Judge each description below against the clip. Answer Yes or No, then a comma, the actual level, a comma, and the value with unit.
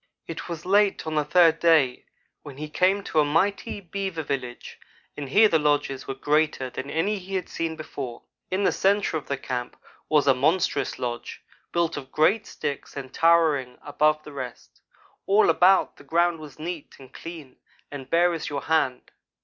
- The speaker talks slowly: No, average, 185 wpm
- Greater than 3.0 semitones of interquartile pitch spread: Yes, average, 3.8 semitones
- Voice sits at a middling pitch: Yes, medium, 155 Hz